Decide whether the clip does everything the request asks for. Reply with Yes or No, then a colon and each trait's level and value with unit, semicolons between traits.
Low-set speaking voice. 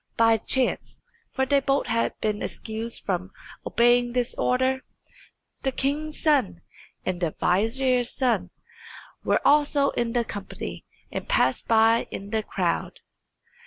No: high, 235 Hz